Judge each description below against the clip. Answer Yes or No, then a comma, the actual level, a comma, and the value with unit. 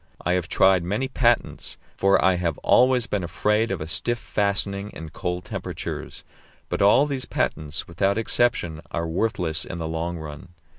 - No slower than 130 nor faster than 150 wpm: No, average, 165 wpm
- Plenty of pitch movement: No, average, 4.5 semitones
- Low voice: Yes, very low, 95 Hz